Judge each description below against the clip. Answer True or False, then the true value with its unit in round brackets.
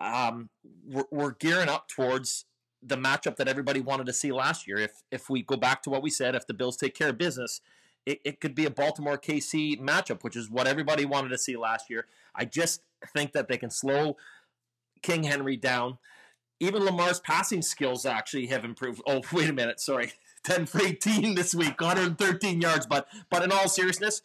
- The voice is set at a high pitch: False (140 Hz)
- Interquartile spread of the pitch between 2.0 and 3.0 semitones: False (4.8 semitones)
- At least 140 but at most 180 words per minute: False (205 wpm)